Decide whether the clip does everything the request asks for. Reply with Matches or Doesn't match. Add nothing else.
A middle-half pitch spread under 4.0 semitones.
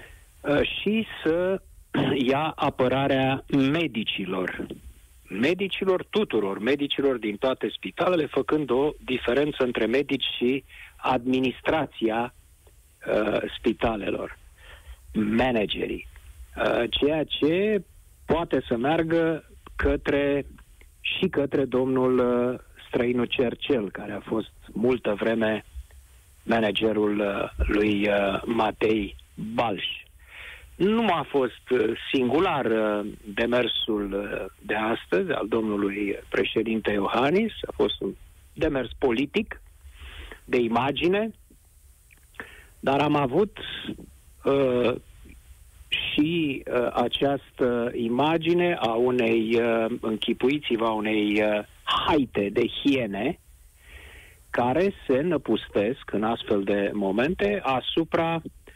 Doesn't match